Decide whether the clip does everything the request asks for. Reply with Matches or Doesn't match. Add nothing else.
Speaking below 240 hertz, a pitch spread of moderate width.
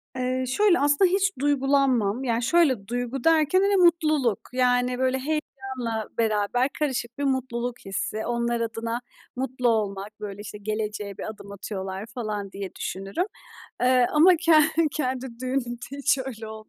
Doesn't match